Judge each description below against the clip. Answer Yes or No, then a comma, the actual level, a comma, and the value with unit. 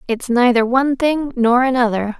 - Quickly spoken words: No, average, 165 wpm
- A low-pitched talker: No, very high, 250 Hz